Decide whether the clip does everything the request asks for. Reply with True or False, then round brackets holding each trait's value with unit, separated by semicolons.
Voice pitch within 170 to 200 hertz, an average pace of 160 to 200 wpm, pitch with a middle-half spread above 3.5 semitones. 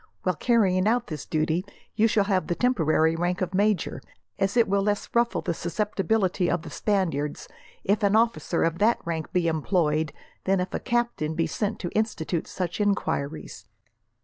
True (185 Hz; 175 wpm; 4.3 semitones)